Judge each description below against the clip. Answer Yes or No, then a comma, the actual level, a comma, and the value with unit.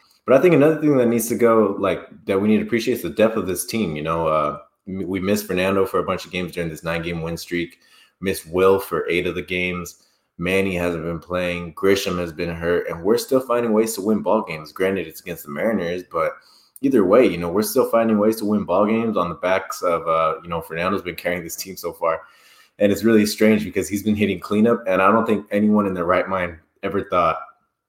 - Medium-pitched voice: No, very low, 95 Hz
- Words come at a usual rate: No, fast, 245 wpm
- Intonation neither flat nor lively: Yes, average, 3.5 semitones